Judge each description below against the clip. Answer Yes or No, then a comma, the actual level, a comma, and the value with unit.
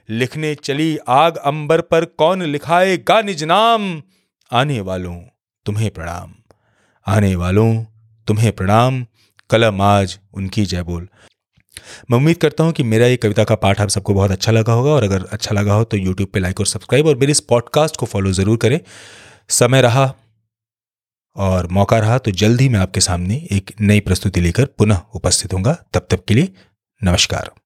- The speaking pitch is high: No, low, 110 Hz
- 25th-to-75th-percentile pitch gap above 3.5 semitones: Yes, average, 5.0 semitones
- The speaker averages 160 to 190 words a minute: Yes, average, 175 wpm